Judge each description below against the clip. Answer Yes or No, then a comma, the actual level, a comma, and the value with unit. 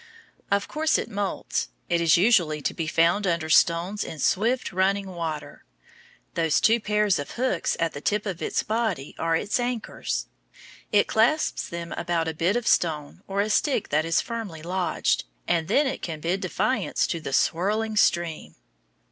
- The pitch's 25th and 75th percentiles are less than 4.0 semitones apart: No, average, 4.4 semitones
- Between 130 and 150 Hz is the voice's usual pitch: No, medium, 185 Hz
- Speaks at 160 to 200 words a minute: Yes, average, 175 wpm